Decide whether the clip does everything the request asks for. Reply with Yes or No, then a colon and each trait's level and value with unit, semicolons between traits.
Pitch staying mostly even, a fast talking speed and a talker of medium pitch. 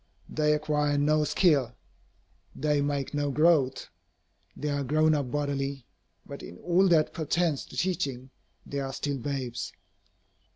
No: narrow, 1.9 semitones; slow, 135 wpm; medium, 145 Hz